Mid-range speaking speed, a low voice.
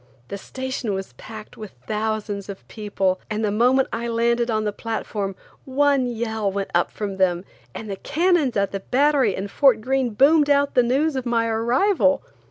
No: average, 180 wpm; high, 230 Hz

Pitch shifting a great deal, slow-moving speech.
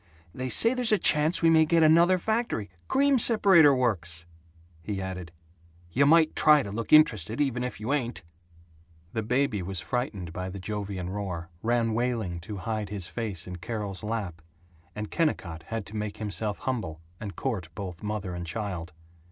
No: wide, 7.0 semitones; average, 170 wpm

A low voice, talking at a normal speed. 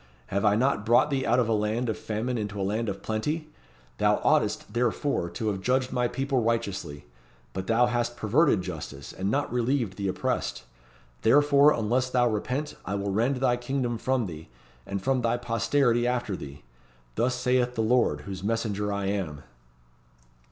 Yes: low, 115 Hz; average, 175 wpm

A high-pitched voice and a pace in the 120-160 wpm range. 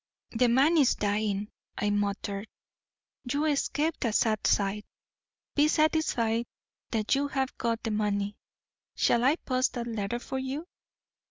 Yes: high, 235 Hz; average, 140 wpm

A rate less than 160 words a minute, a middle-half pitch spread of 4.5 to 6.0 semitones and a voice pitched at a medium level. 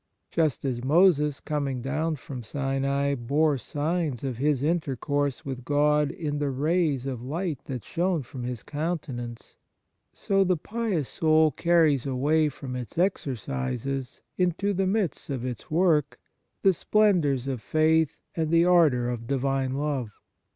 No: average, 145 wpm; average, 3.7 semitones; medium, 145 Hz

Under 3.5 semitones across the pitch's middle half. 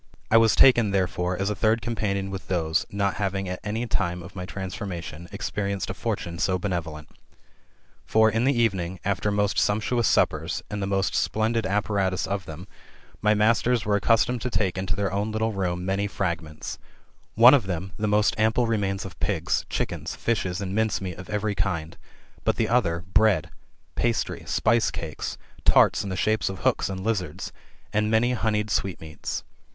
Yes: average, 2.9 semitones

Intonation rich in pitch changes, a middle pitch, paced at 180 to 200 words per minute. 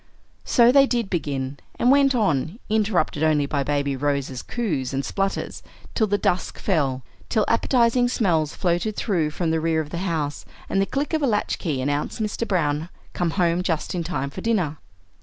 Yes: wide, 6.8 semitones; medium, 170 Hz; average, 185 wpm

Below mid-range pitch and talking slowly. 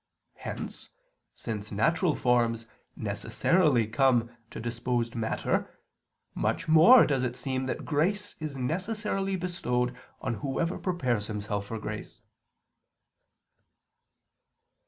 Yes: low, 130 Hz; slow, 100 wpm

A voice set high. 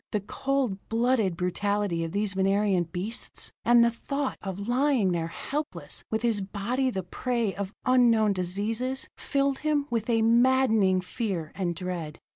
Yes: high, 210 Hz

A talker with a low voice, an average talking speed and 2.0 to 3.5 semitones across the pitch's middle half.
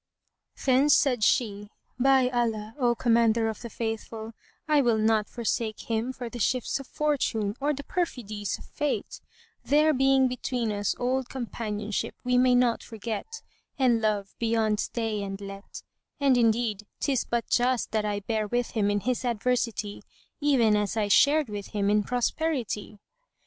No: high, 235 Hz; average, 160 wpm; average, 3.1 semitones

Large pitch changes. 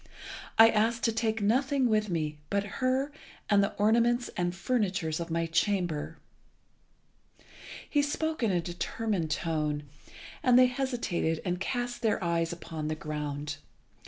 Yes: wide, 6.5 semitones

